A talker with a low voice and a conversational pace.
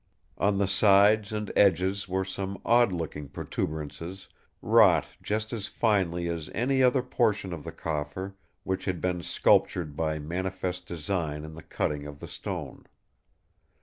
Yes: very low, 95 Hz; average, 150 wpm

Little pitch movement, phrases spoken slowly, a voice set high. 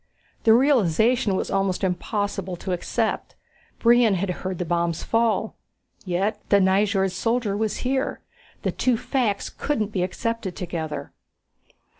No: average, 3.8 semitones; slow, 130 wpm; high, 200 Hz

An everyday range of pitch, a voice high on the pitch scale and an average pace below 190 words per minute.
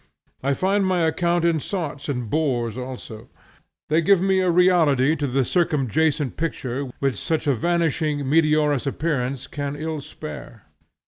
No: average, 3.6 semitones; medium, 150 Hz; average, 140 wpm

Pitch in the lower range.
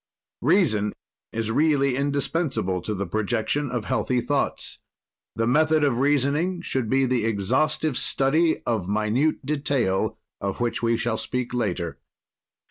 Yes: low, 125 Hz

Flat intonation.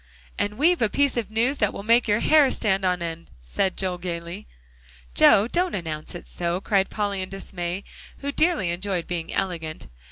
No: average, 4.5 semitones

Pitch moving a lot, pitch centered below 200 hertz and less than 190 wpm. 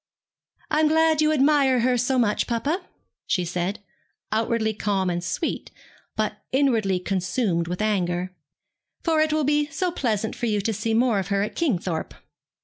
No: wide, 6.8 semitones; high, 225 Hz; average, 165 wpm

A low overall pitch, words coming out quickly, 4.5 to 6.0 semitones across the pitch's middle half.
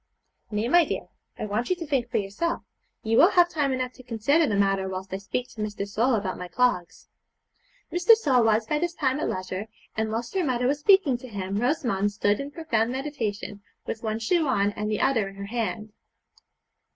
No: high, 230 Hz; fast, 210 wpm; wide, 5.6 semitones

